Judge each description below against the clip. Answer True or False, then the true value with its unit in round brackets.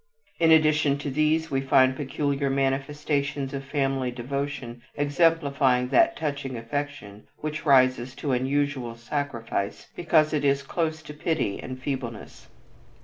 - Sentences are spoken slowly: True (130 wpm)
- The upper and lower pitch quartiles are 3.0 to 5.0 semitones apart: False (2.4 semitones)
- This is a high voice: False (140 Hz)